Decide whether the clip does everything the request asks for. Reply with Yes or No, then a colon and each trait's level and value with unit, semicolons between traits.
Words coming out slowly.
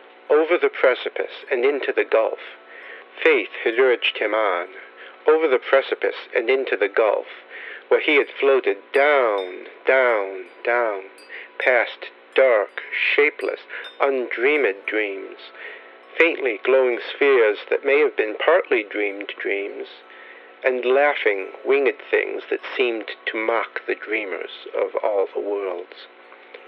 Yes: slow, 125 wpm